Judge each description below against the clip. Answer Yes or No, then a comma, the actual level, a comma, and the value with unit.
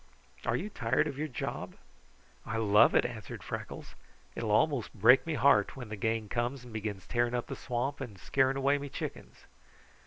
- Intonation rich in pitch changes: No, average, 3.7 semitones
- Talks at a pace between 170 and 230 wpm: Yes, average, 190 wpm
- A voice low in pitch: Yes, low, 120 Hz